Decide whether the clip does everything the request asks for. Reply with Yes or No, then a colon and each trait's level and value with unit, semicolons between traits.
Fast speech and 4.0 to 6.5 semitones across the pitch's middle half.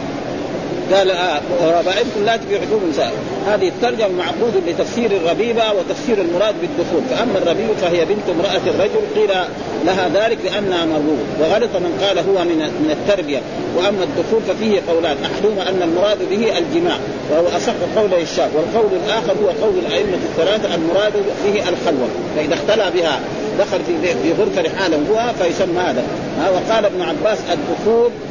Yes: fast, 140 wpm; average, 4.3 semitones